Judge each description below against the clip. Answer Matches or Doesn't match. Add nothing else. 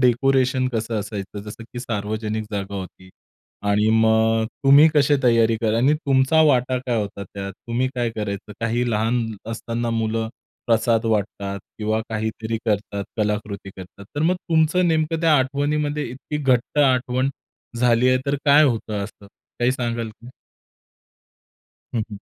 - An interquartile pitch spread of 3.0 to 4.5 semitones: Matches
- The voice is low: Matches